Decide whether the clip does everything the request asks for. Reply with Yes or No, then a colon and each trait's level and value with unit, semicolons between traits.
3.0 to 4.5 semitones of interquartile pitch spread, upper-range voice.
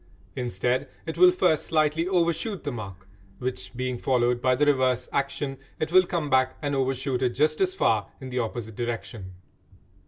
No: average, 4.2 semitones; low, 130 Hz